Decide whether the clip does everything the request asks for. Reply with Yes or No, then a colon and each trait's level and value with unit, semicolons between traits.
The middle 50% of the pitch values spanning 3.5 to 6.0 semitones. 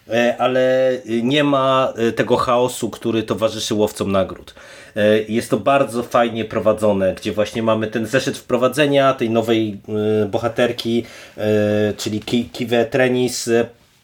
No: narrow, 2.4 semitones